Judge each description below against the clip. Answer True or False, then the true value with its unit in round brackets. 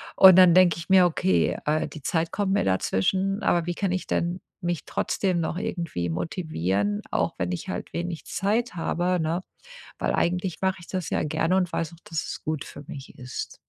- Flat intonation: False (3.2 semitones)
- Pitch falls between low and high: True (170 Hz)